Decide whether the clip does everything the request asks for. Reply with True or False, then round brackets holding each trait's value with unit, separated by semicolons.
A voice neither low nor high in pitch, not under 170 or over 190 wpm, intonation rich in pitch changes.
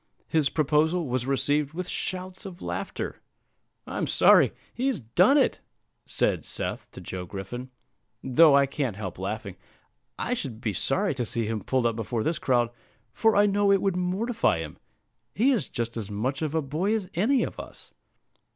True (150 Hz; 175 wpm; 8.2 semitones)